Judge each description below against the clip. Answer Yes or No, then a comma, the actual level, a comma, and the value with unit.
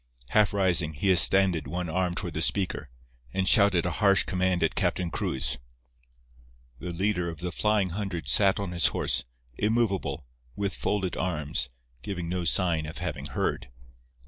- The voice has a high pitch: No, very low, 90 Hz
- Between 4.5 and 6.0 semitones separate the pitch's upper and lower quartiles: No, average, 2.9 semitones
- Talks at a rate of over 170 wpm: No, average, 150 wpm